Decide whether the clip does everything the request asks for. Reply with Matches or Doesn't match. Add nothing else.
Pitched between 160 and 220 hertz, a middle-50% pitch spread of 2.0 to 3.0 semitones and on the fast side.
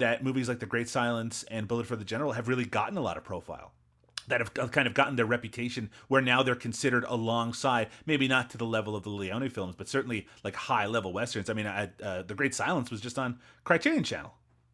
Doesn't match